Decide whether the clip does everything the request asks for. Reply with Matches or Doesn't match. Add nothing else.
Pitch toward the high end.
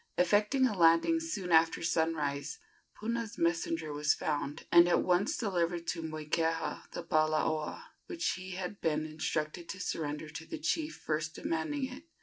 Doesn't match